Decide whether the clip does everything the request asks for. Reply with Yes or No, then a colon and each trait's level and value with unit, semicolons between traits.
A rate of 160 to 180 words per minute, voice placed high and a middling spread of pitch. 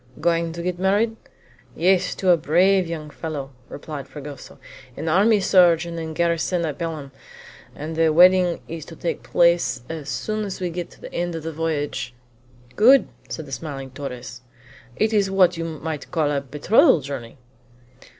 No: average, 170 wpm; medium, 165 Hz; average, 3.4 semitones